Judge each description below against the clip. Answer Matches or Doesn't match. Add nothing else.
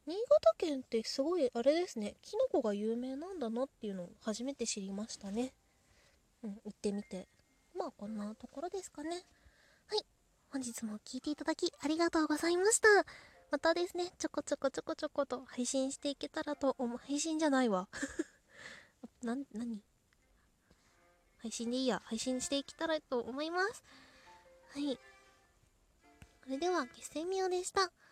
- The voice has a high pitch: Matches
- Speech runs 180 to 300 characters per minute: Doesn't match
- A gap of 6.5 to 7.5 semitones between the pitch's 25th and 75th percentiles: Doesn't match